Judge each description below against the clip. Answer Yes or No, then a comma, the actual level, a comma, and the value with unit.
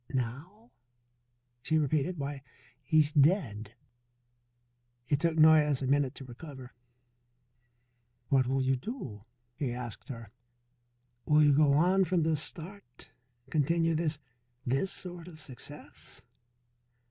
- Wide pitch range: No, average, 3.9 semitones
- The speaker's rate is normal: No, slow, 120 wpm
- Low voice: No, medium, 150 Hz